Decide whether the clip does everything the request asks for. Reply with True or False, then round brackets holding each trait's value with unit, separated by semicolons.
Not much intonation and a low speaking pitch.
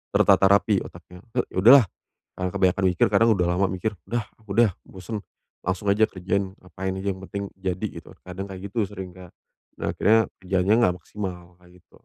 True (2.0 semitones; 95 Hz)